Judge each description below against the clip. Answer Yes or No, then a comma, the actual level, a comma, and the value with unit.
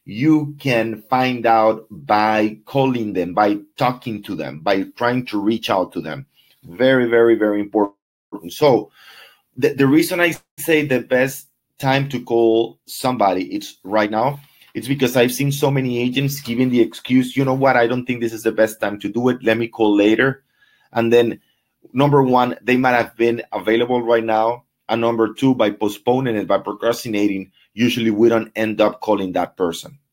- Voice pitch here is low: Yes, low, 120 Hz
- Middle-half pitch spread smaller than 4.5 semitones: Yes, average, 2.9 semitones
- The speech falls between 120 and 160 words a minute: No, average, 185 wpm